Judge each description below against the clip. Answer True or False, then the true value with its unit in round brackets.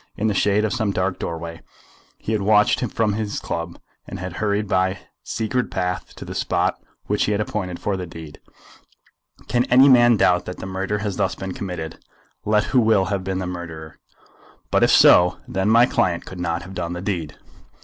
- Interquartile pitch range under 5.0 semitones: True (3.1 semitones)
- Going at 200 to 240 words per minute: True (205 wpm)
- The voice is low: True (95 Hz)